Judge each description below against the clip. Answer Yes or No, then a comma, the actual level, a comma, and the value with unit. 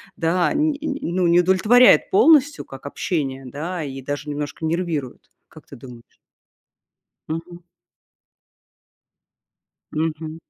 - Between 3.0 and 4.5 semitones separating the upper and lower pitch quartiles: Yes, average, 4.2 semitones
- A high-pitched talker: No, medium, 165 Hz